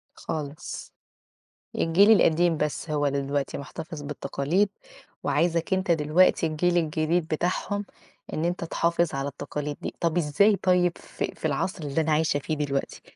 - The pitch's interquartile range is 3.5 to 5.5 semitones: No, average, 3.0 semitones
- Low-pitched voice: No, medium, 160 Hz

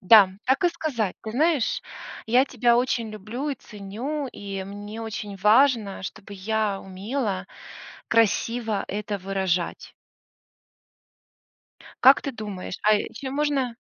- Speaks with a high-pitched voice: Yes, high, 220 Hz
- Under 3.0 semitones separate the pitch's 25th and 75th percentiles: No, average, 4.2 semitones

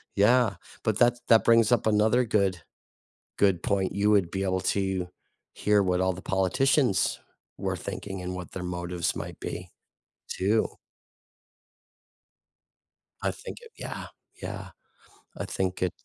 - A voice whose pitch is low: Yes, low, 100 Hz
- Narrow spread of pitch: No, average, 3.0 semitones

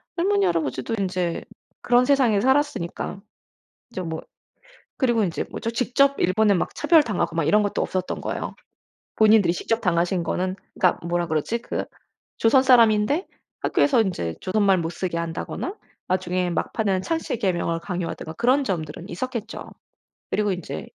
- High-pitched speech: Yes, high, 200 Hz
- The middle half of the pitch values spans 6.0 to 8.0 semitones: No, wide, 5.5 semitones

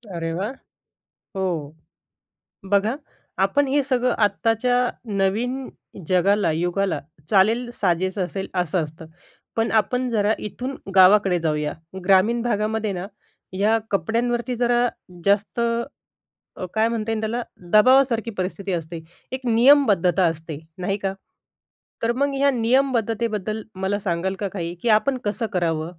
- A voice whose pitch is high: Yes, high, 210 Hz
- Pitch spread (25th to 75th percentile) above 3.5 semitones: Yes, average, 4.2 semitones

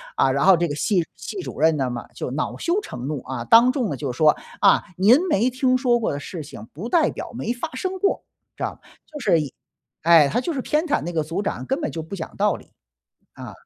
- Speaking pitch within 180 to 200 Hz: Yes, high, 190 Hz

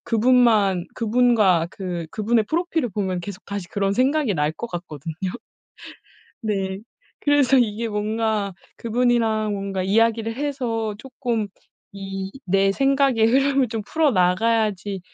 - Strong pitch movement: No, average, 3.8 semitones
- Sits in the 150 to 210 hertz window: No, high, 220 Hz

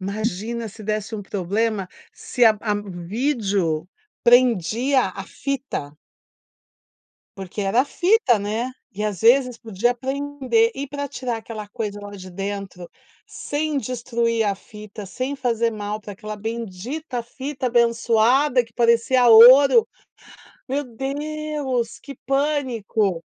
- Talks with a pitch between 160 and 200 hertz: No, high, 230 Hz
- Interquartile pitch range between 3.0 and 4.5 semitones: Yes, average, 4.2 semitones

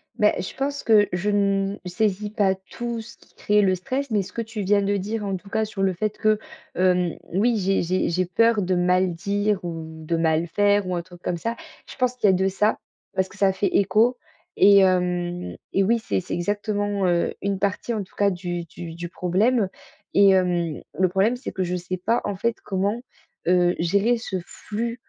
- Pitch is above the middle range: Yes, high, 195 Hz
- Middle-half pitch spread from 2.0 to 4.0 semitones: Yes, average, 2.8 semitones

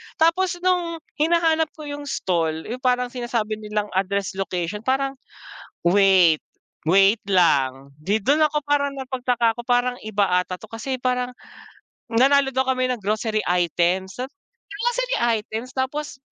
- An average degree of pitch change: No, wide, 5.9 semitones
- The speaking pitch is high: Yes, high, 240 Hz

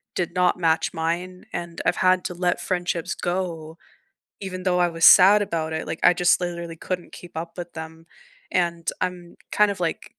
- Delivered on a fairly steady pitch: Yes, narrow, 1.6 semitones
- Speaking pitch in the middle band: Yes, medium, 175 Hz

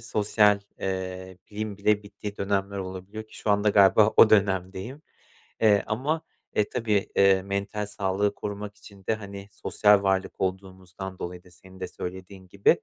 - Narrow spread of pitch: Yes, narrow, 1.7 semitones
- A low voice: Yes, low, 100 Hz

